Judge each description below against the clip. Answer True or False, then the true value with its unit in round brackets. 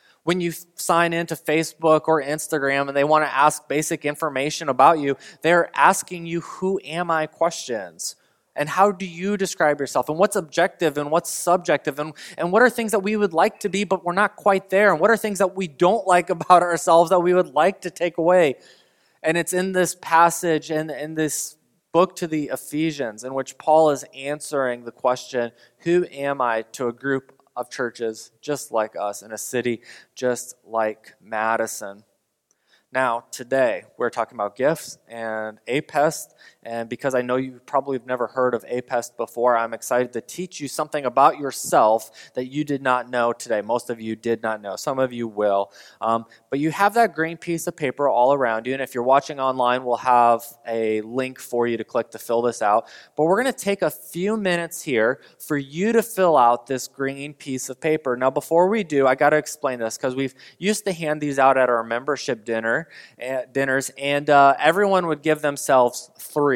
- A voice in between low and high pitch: True (145 Hz)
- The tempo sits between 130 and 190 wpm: False (205 wpm)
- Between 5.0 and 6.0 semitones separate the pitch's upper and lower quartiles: True (5.6 semitones)